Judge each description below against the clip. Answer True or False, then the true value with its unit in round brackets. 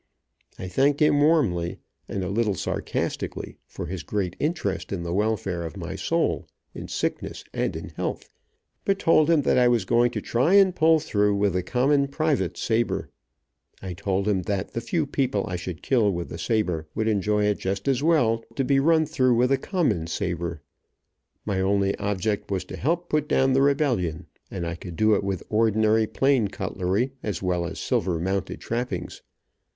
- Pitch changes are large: True (6.4 semitones)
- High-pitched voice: False (105 Hz)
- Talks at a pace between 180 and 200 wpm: True (185 wpm)